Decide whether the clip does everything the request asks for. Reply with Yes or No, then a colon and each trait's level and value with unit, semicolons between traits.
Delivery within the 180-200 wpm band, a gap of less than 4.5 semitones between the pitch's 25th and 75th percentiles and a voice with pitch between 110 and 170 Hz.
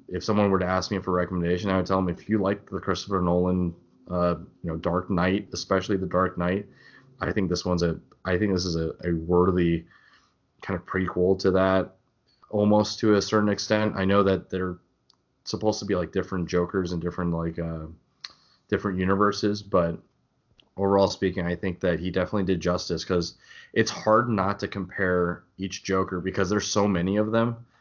No: average, 195 wpm; narrow, 2.5 semitones; very low, 95 Hz